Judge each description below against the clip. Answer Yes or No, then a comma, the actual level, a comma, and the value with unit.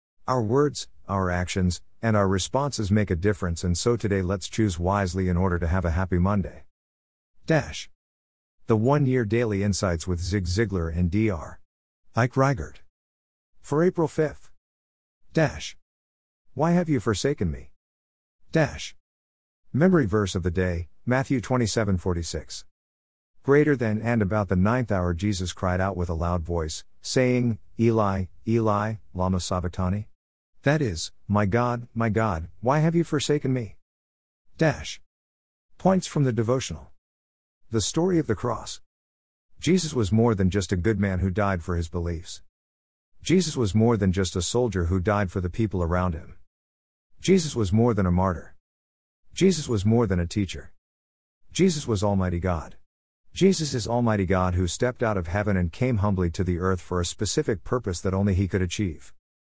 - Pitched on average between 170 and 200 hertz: No, very low, 95 Hz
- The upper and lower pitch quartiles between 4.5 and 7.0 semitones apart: Yes, wide, 5.6 semitones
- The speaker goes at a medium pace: Yes, average, 160 wpm